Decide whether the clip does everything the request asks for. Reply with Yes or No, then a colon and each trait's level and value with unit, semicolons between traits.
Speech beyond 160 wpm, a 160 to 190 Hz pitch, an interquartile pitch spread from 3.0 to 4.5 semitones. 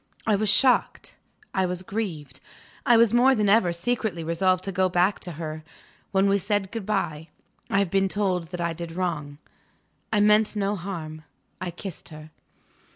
Yes: average, 175 wpm; medium, 185 Hz; average, 3.5 semitones